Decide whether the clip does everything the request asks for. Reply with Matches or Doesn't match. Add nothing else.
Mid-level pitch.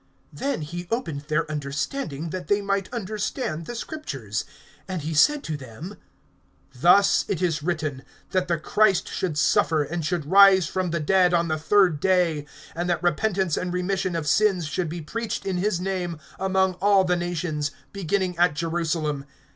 Matches